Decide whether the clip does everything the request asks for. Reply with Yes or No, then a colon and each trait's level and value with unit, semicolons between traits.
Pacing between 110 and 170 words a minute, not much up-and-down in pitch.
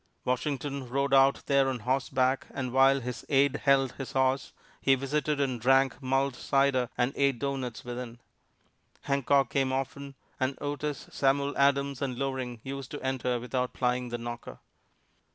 Yes: average, 150 wpm; narrow, 1.6 semitones